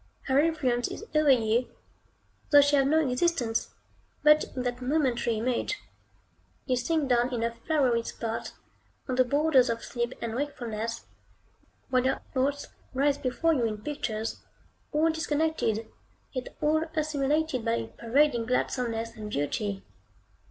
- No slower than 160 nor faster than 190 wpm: No, average, 140 wpm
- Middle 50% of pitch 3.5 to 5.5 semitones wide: Yes, average, 4.2 semitones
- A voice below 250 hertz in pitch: No, very high, 255 Hz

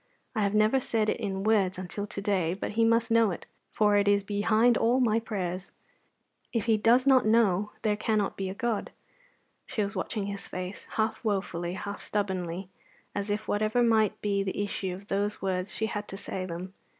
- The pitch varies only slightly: Yes, narrow, 2.3 semitones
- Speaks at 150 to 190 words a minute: No, average, 200 wpm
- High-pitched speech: Yes, high, 205 Hz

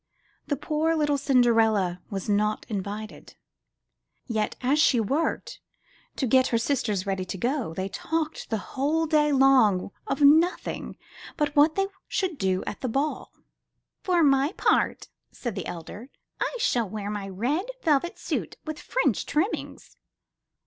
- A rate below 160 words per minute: Yes, average, 140 wpm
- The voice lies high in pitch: Yes, very high, 260 Hz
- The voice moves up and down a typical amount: No, wide, 6.5 semitones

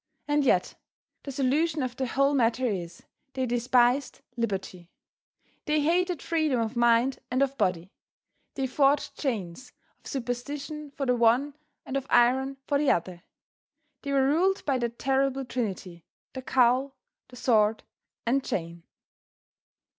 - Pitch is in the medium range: No, very high, 255 Hz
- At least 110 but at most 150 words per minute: Yes, average, 140 wpm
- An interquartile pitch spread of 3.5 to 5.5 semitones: No, average, 3.1 semitones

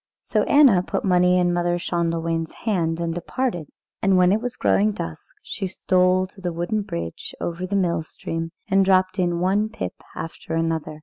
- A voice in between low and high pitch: Yes, medium, 180 Hz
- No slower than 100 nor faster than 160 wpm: No, average, 180 wpm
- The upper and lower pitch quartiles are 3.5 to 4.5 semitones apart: No, narrow, 2.6 semitones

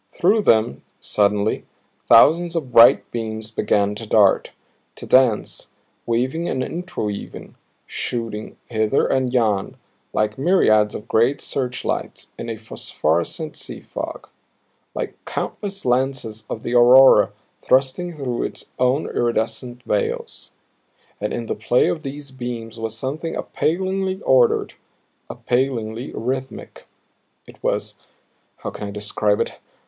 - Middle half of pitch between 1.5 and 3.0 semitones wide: No, average, 3.6 semitones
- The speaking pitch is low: Yes, low, 120 Hz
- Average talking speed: No, slow, 125 wpm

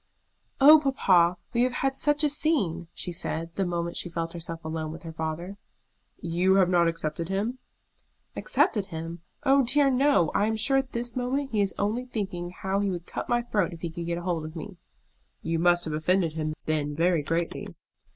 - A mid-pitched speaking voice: Yes, medium, 180 Hz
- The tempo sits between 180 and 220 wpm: Yes, average, 200 wpm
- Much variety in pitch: Yes, wide, 6.2 semitones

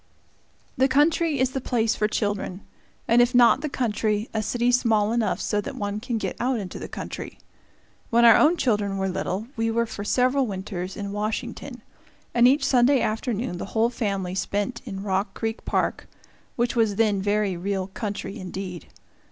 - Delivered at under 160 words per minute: No, average, 175 wpm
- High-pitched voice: Yes, high, 220 Hz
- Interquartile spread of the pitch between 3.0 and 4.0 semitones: Yes, average, 3.3 semitones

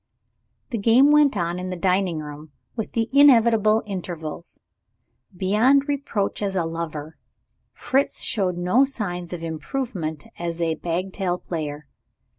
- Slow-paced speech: Yes, slow, 130 wpm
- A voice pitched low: No, medium, 185 Hz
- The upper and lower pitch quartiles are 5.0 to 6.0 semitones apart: Yes, average, 5.3 semitones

